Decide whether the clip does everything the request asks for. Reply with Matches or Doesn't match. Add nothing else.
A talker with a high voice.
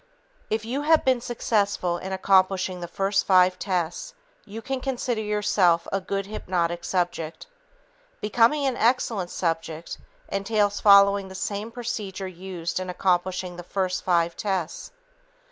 Matches